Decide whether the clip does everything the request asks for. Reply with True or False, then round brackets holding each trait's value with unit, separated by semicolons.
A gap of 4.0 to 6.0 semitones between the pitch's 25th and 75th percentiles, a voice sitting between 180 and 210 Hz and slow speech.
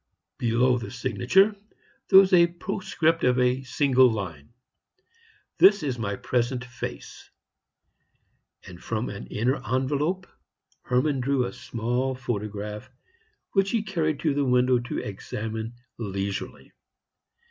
False (4.8 semitones; 125 Hz; 120 wpm)